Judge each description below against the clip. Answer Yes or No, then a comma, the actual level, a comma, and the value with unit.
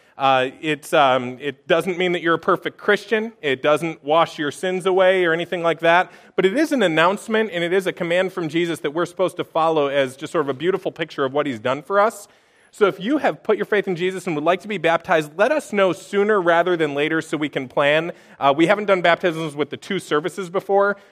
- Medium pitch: Yes, medium, 175 Hz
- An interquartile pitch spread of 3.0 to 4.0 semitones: Yes, average, 3.5 semitones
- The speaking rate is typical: No, fast, 245 wpm